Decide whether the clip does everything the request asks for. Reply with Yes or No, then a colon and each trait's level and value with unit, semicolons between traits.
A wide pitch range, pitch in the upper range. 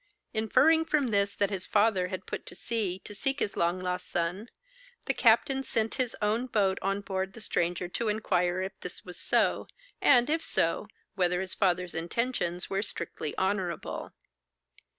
No: average, 3.8 semitones; high, 195 Hz